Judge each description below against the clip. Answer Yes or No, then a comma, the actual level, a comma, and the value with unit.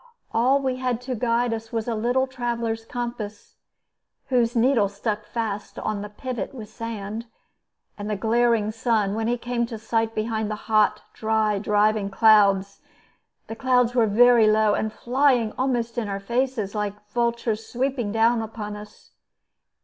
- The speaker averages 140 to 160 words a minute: Yes, average, 155 wpm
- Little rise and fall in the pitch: Yes, narrow, 2.3 semitones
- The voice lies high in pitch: Yes, high, 225 Hz